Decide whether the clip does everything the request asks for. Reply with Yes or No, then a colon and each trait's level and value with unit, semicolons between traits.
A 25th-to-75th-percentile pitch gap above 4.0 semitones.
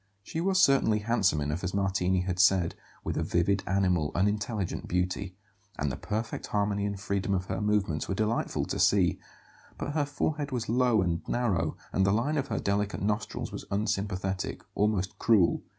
No: average, 2.9 semitones